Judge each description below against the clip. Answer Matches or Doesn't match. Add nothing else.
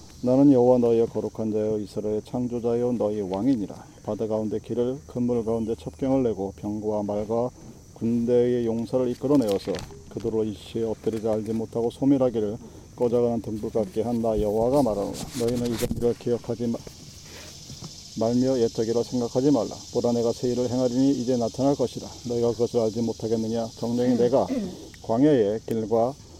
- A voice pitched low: Matches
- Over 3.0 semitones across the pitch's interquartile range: Doesn't match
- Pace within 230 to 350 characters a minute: Doesn't match